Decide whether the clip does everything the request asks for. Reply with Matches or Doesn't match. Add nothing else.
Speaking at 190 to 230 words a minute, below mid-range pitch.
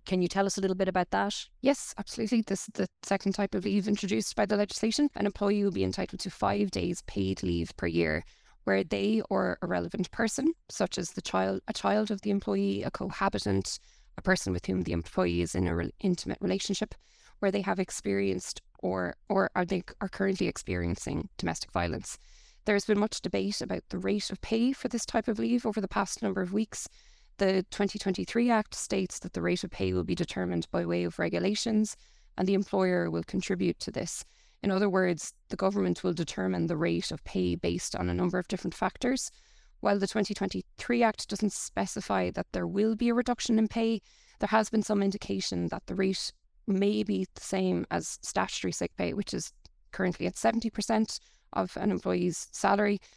Doesn't match